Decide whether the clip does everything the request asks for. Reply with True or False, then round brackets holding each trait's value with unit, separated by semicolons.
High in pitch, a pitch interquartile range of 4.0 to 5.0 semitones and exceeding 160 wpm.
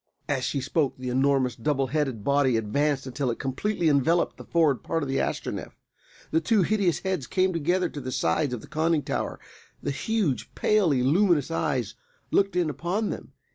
False (145 Hz; 4.6 semitones; 180 wpm)